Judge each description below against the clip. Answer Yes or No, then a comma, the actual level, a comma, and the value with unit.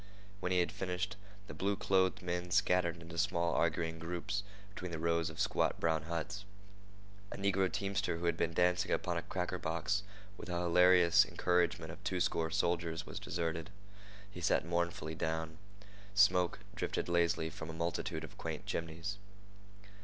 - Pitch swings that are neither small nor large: No, narrow, 1.8 semitones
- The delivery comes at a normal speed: Yes, average, 160 wpm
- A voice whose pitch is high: No, very low, 85 Hz